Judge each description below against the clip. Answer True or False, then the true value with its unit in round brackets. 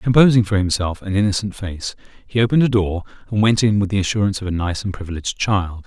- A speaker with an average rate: False (225 wpm)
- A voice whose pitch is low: True (100 Hz)